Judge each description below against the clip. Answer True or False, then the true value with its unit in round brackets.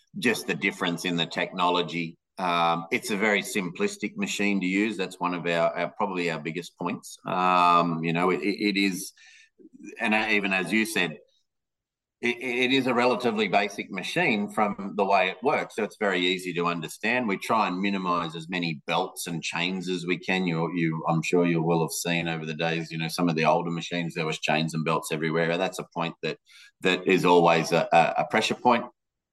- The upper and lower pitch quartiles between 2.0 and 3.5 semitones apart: True (3.2 semitones)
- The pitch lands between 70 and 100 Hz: True (90 Hz)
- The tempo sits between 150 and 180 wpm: False (205 wpm)